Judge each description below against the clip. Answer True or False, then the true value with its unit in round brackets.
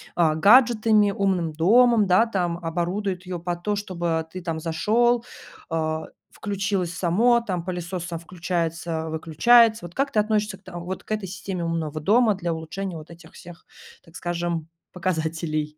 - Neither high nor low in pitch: True (180 Hz)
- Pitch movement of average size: True (3.7 semitones)